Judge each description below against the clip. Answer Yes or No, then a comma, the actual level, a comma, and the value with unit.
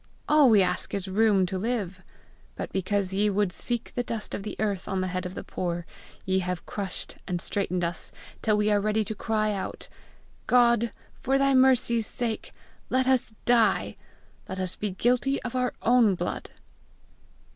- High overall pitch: Yes, high, 210 Hz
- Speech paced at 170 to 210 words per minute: Yes, average, 180 wpm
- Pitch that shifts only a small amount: No, average, 4.0 semitones